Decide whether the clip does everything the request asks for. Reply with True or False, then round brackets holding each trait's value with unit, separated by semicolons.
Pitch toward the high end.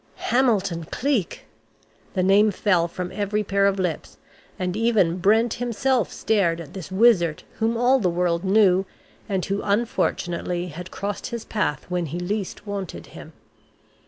True (195 Hz)